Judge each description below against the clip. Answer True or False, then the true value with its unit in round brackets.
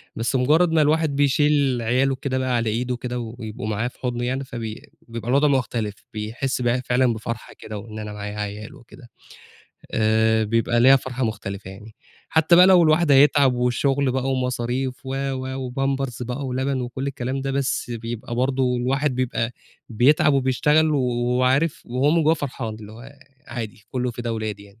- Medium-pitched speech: False (125 Hz)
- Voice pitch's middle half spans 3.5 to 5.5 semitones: False (3.0 semitones)